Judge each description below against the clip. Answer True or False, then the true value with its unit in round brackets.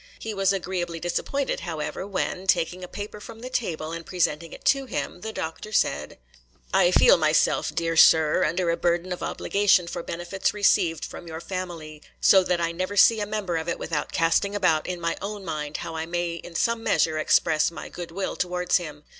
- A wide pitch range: False (2.8 semitones)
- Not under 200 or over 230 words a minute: True (205 wpm)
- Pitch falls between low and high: True (175 Hz)